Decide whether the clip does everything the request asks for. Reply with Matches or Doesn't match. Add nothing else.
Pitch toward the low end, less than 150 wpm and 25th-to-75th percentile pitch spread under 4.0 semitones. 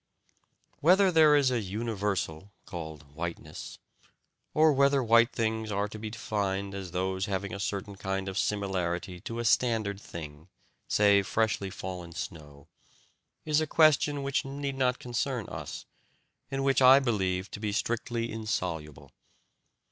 Doesn't match